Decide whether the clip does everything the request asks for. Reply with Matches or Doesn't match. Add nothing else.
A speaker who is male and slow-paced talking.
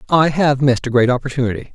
Doesn't match